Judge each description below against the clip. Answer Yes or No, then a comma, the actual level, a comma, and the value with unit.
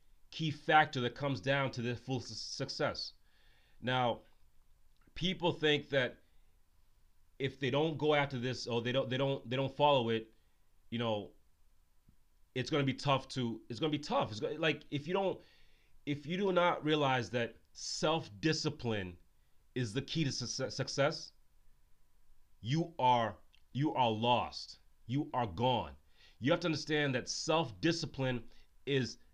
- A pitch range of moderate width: No, wide, 6.6 semitones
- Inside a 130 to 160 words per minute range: Yes, average, 150 wpm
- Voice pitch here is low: Yes, low, 125 Hz